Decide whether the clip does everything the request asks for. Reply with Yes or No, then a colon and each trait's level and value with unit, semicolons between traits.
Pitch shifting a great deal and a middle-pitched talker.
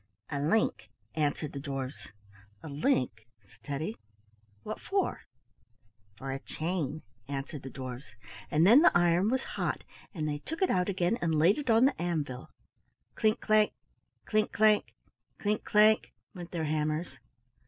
Yes: wide, 7.0 semitones; medium, 165 Hz